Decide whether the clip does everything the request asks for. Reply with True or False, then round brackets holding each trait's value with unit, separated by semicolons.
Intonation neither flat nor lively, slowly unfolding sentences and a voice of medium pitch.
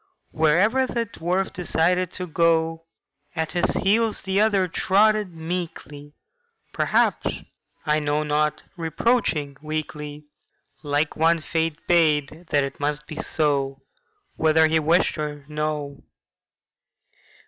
True (3.2 semitones; 105 wpm; 160 Hz)